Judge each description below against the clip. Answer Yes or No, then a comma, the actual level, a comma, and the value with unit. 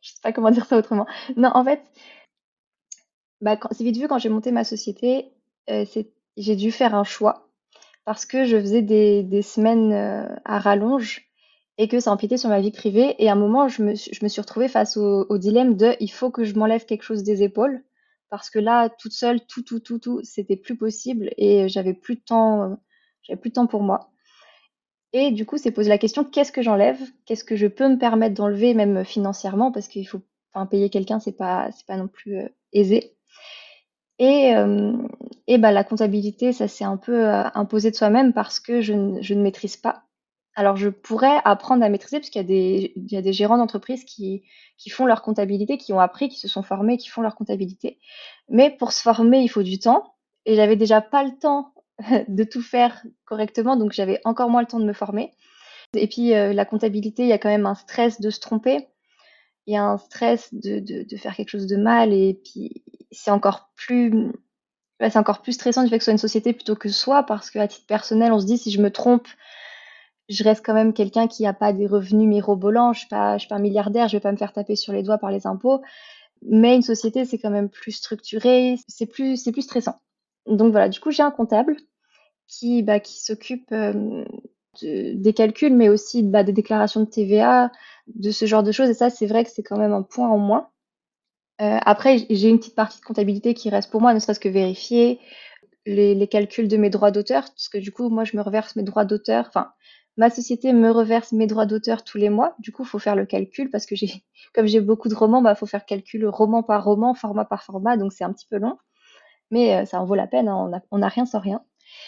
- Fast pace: Yes, fast, 235 wpm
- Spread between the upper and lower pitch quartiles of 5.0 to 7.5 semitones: No, average, 2.8 semitones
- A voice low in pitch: No, high, 220 Hz